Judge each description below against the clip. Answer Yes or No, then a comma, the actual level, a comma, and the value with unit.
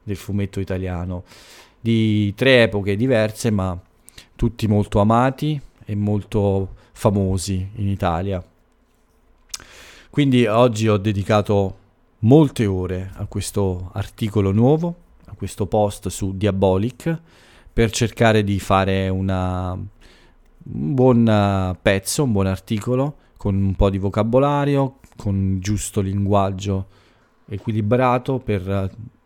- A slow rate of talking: Yes, slow, 105 wpm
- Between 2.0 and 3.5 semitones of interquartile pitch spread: Yes, average, 2.9 semitones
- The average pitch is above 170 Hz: No, low, 105 Hz